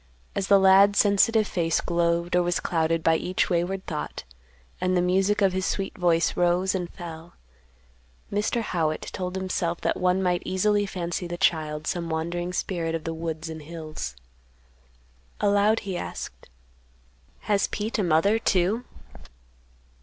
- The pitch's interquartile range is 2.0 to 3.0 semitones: Yes, average, 2.7 semitones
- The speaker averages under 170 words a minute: Yes, average, 150 wpm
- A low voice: No, medium, 180 Hz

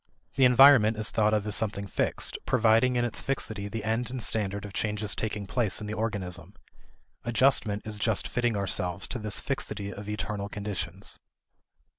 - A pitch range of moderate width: No, narrow, 2.2 semitones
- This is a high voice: No, low, 105 Hz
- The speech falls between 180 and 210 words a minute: No, average, 170 wpm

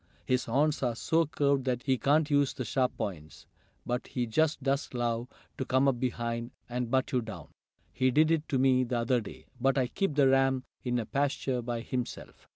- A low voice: Yes, low, 130 Hz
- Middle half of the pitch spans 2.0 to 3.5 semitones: Yes, narrow, 2.4 semitones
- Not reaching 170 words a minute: No, fast, 205 wpm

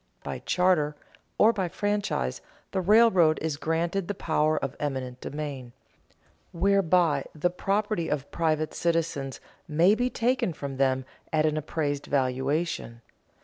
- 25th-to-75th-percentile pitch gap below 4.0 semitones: No, average, 4.5 semitones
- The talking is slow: Yes, slow, 130 wpm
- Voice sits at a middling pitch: Yes, medium, 155 Hz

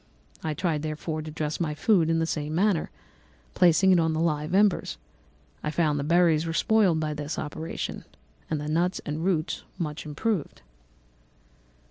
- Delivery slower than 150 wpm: No, average, 170 wpm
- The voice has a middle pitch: Yes, medium, 160 Hz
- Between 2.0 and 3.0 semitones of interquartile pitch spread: Yes, narrow, 2.4 semitones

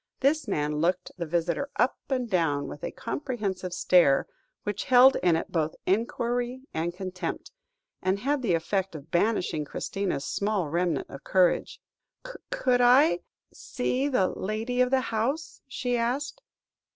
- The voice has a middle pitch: No, high, 205 Hz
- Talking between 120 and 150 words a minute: Yes, average, 145 wpm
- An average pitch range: No, wide, 6.5 semitones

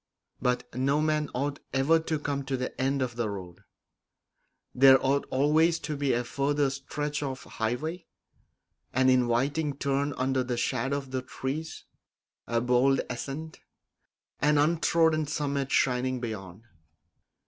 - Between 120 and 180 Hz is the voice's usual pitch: Yes, low, 135 Hz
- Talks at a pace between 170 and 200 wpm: No, slow, 135 wpm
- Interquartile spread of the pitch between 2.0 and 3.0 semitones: Yes, average, 2.7 semitones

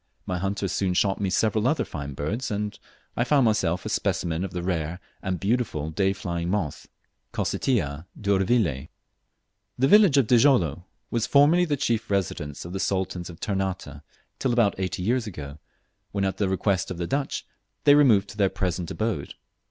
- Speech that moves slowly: No, average, 175 wpm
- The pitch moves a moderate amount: Yes, average, 4.7 semitones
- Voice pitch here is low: Yes, very low, 95 Hz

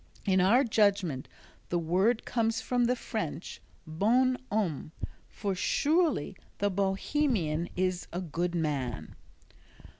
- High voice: Yes, high, 195 Hz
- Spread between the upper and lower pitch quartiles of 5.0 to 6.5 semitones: Yes, average, 5.3 semitones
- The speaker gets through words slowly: Yes, slow, 115 wpm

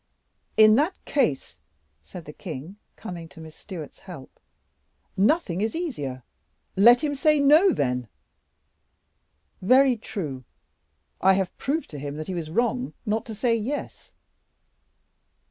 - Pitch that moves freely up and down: Yes, wide, 8.6 semitones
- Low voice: No, high, 205 Hz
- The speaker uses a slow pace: Yes, slow, 130 wpm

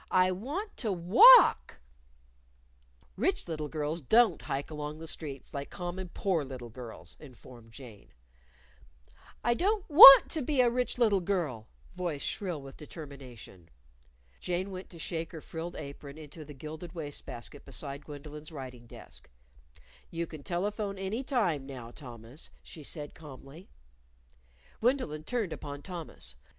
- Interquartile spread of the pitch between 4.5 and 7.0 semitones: Yes, average, 5.3 semitones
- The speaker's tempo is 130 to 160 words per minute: Yes, average, 140 wpm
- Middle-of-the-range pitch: Yes, medium, 160 Hz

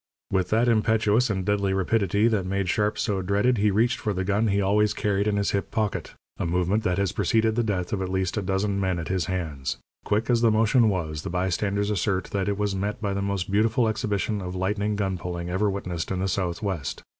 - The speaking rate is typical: No, fast, 225 wpm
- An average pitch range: No, narrow, 2.2 semitones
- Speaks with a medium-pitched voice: No, low, 100 Hz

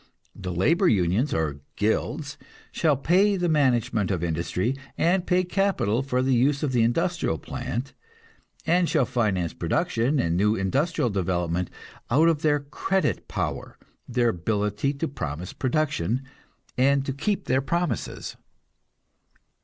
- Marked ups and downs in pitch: Yes, wide, 7.5 semitones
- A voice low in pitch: Yes, low, 130 Hz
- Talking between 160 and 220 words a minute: No, slow, 135 wpm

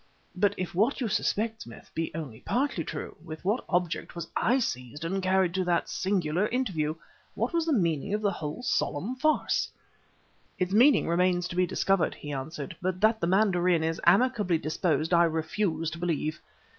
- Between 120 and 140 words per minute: No, average, 180 wpm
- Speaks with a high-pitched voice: No, medium, 180 Hz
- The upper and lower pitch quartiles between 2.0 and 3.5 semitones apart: No, average, 4.2 semitones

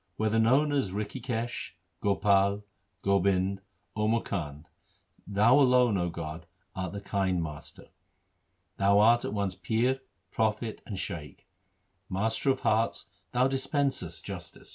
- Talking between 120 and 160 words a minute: Yes, slow, 135 wpm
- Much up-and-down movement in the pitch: No, average, 3.8 semitones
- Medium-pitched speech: No, low, 105 Hz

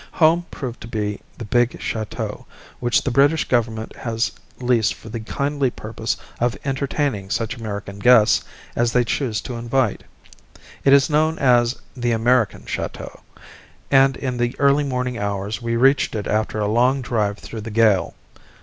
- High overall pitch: No, low, 120 Hz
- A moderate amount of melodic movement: Yes, average, 3.2 semitones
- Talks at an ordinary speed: Yes, average, 160 wpm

